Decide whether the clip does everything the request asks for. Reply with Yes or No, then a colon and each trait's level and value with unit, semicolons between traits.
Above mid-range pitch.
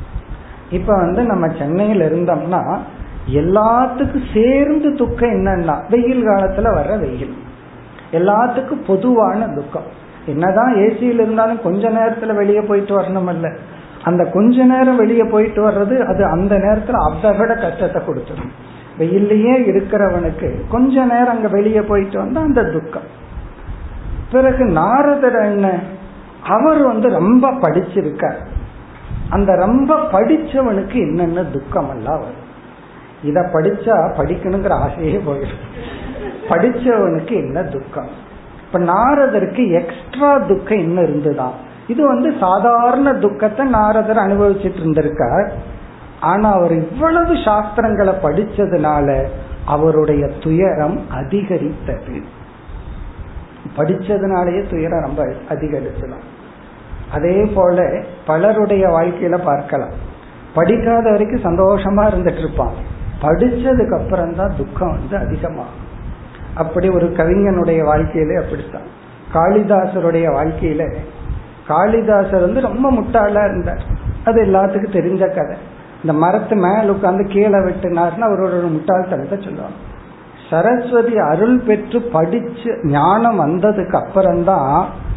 Yes: high, 195 Hz